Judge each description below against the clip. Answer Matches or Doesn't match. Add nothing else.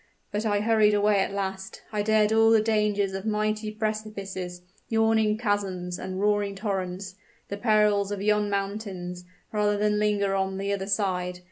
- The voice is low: Doesn't match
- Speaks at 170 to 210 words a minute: Doesn't match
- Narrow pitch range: Matches